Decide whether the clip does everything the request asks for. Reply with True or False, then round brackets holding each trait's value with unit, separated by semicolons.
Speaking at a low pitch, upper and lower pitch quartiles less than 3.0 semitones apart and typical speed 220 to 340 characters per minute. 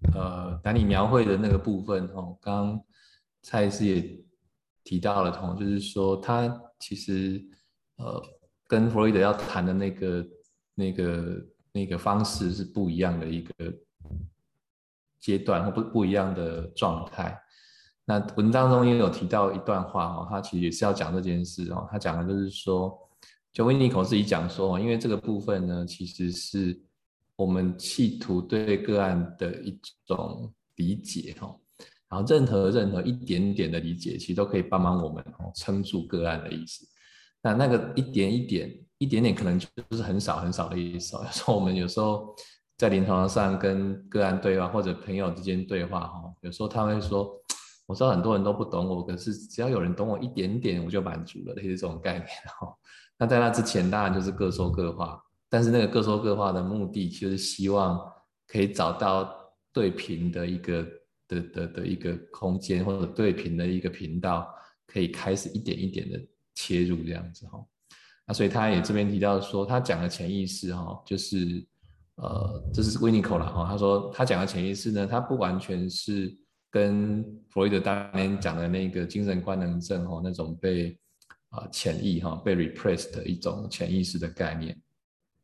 True (95 Hz; 2.5 semitones; 275 characters per minute)